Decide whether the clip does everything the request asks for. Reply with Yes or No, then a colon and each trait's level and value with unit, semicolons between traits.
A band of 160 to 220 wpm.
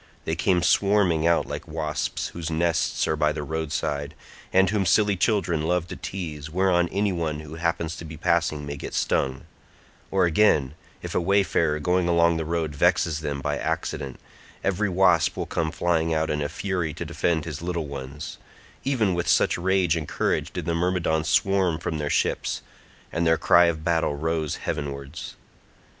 Yes: average, 175 wpm